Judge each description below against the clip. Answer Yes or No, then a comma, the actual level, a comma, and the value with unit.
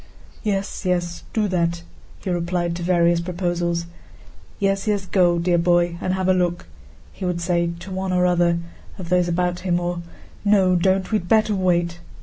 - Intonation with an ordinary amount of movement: No, narrow, 1.5 semitones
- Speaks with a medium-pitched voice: Yes, medium, 180 Hz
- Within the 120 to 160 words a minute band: No, average, 170 wpm